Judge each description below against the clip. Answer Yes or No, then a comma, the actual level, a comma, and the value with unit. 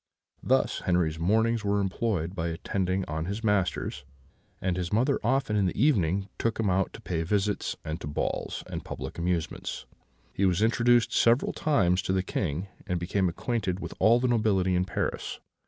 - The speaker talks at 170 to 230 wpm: Yes, average, 175 wpm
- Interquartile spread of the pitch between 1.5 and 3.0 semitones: No, average, 3.9 semitones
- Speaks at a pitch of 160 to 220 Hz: No, very low, 95 Hz